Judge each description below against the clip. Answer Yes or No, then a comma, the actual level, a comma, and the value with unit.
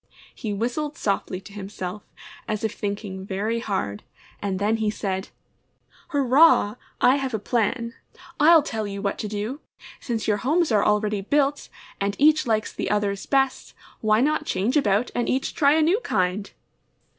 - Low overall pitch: No, high, 215 Hz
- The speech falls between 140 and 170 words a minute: Yes, average, 165 wpm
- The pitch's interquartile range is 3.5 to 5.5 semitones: Yes, average, 5.1 semitones